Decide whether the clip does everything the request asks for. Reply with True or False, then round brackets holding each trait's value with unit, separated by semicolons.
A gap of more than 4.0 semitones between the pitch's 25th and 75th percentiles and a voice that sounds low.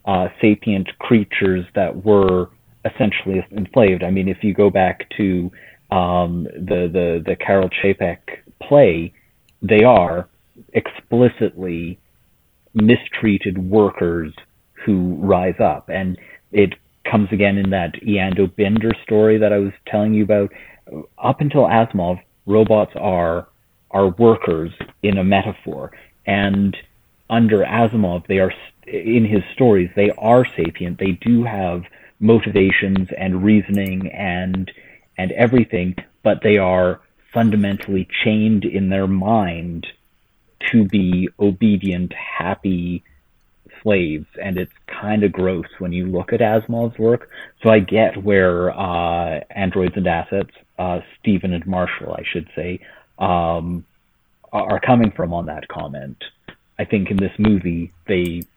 False (2.8 semitones; 95 Hz)